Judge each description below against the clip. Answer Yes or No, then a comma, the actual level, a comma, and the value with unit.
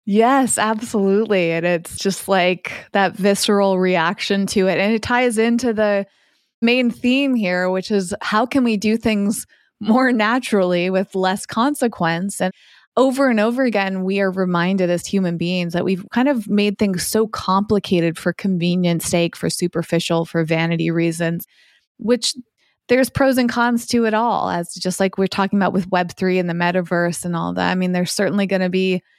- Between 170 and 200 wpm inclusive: Yes, average, 180 wpm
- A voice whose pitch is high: Yes, high, 195 Hz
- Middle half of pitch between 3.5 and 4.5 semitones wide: Yes, average, 3.8 semitones